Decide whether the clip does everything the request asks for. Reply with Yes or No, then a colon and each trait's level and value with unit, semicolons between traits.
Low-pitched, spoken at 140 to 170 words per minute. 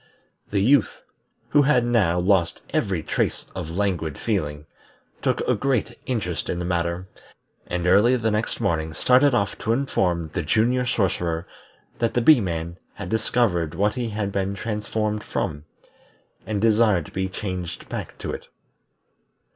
Yes: low, 100 Hz; average, 155 wpm